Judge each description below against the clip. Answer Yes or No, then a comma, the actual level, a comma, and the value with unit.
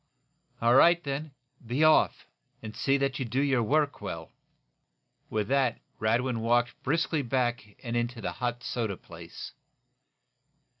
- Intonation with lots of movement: No, average, 3.1 semitones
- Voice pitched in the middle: No, low, 125 Hz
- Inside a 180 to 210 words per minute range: No, average, 140 wpm